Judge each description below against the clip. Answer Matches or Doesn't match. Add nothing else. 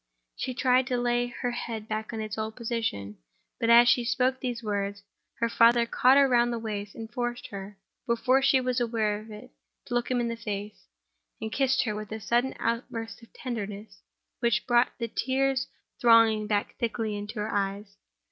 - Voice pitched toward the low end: Doesn't match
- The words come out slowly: Doesn't match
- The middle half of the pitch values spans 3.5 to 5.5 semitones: Doesn't match